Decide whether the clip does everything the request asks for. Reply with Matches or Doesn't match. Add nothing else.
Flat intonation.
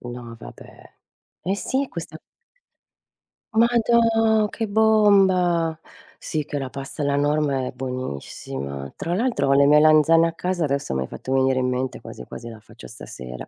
Doesn't match